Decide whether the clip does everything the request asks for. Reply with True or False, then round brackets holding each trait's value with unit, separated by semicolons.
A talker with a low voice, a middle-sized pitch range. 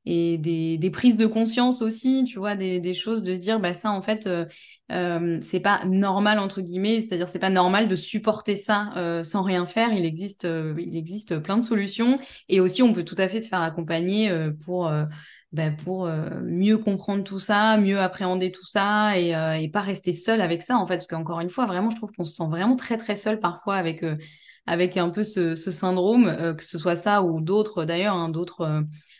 False (185 Hz; 3.6 semitones)